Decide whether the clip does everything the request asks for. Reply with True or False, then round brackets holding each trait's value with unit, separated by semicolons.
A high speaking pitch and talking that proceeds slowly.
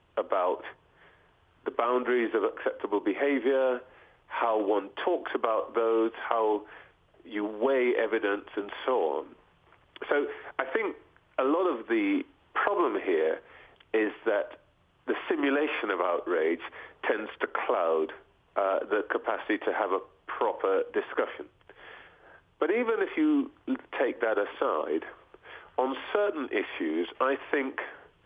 True (345 Hz; 120 wpm)